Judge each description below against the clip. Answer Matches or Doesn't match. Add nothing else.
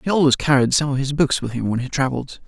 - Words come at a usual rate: Doesn't match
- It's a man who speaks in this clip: Matches